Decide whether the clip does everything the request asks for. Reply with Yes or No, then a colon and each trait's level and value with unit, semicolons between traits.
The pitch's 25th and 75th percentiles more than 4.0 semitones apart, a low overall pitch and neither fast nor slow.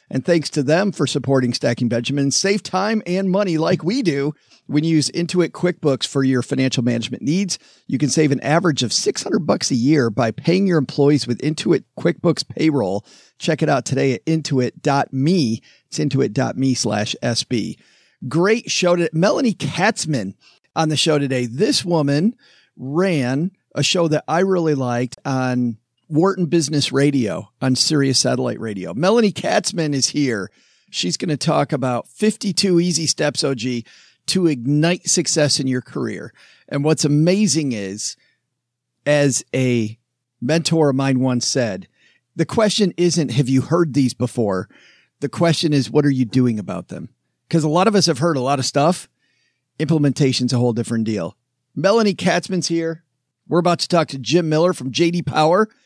No: average, 4.8 semitones; medium, 145 Hz; average, 165 wpm